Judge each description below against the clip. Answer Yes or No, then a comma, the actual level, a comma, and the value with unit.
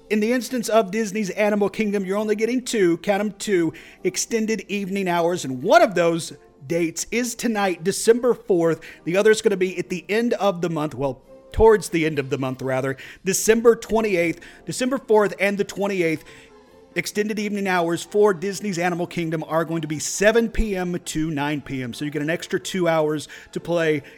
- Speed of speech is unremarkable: Yes, average, 195 wpm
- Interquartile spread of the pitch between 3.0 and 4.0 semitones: No, average, 4.6 semitones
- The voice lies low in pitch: No, medium, 185 Hz